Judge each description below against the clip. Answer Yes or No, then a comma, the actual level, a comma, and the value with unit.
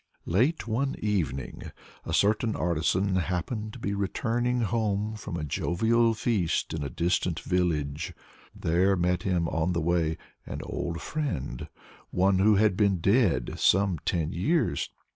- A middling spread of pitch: Yes, average, 4.5 semitones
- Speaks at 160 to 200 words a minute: No, average, 140 wpm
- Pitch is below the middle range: Yes, very low, 95 Hz